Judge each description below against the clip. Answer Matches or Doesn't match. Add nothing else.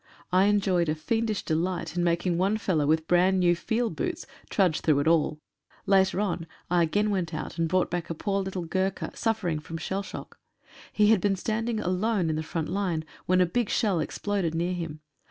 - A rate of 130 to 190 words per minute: Doesn't match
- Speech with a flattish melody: Doesn't match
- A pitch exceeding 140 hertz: Matches